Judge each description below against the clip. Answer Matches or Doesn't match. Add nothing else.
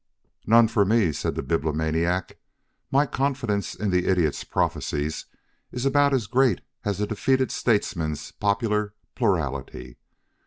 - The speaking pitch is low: Matches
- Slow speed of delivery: Matches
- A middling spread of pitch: Doesn't match